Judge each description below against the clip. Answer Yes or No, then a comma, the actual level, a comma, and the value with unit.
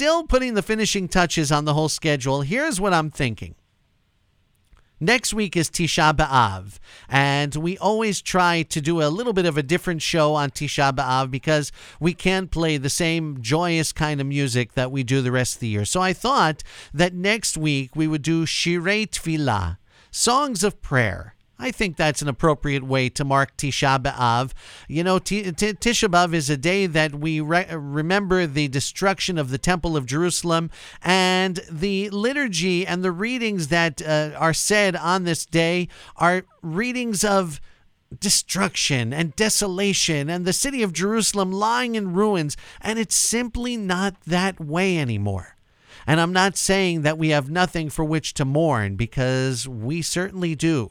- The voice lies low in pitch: No, medium, 165 Hz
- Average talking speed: Yes, average, 170 wpm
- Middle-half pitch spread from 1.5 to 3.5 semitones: No, average, 4.9 semitones